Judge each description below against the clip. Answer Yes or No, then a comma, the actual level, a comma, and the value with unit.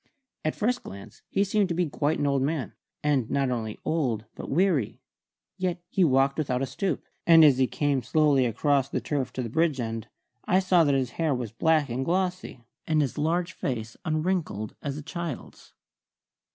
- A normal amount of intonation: Yes, average, 4.7 semitones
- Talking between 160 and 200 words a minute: Yes, average, 190 wpm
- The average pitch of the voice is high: No, medium, 145 Hz